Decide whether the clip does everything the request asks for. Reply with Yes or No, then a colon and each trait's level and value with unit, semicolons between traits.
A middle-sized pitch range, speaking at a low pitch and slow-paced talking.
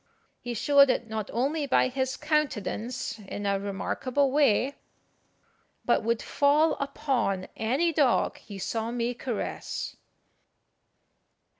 No: average, 4.2 semitones; very high, 250 Hz; slow, 115 wpm